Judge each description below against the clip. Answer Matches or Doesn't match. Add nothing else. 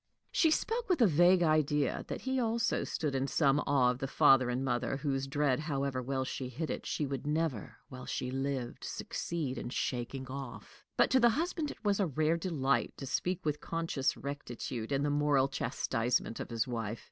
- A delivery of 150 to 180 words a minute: Doesn't match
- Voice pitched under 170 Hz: Matches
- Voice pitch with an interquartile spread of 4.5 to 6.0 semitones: Doesn't match